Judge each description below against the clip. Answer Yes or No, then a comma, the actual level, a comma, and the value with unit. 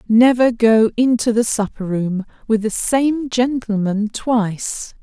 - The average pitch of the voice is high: Yes, high, 225 Hz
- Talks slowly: Yes, slow, 130 wpm